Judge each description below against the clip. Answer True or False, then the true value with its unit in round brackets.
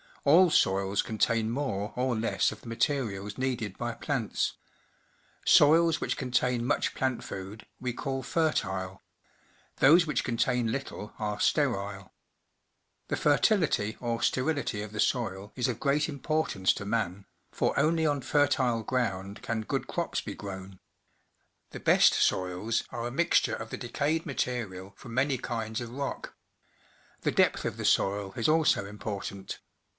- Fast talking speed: False (145 wpm)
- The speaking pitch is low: True (120 Hz)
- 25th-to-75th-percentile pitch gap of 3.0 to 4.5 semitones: False (5.2 semitones)